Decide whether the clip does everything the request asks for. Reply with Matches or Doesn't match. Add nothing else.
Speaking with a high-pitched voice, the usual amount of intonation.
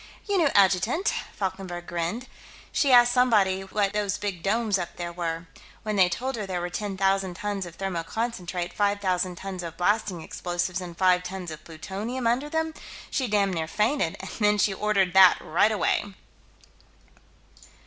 Matches